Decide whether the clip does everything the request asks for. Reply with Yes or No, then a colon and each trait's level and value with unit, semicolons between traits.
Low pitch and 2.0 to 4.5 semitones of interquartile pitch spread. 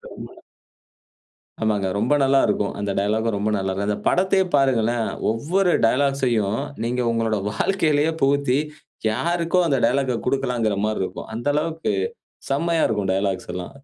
No: low, 120 Hz; average, 5.0 semitones